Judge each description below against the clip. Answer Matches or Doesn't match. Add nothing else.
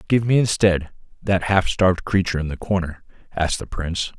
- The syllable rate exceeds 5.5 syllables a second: Matches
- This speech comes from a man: Matches